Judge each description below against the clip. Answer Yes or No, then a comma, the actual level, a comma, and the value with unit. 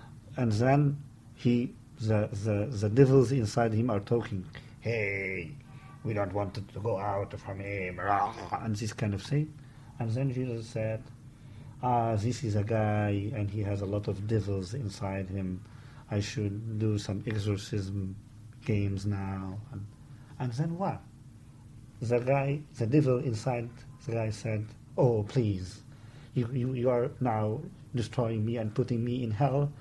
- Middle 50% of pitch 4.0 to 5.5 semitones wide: No, average, 3.6 semitones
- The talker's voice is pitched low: Yes, low, 115 Hz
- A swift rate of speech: No, average, 155 wpm